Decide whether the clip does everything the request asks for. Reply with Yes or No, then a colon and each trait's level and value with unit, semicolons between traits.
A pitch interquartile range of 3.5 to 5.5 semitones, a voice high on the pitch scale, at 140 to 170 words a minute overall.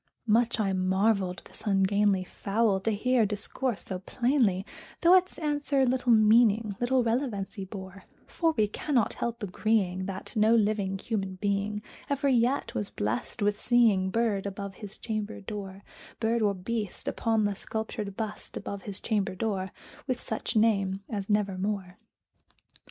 No: average, 3.0 semitones; high, 210 Hz; average, 145 wpm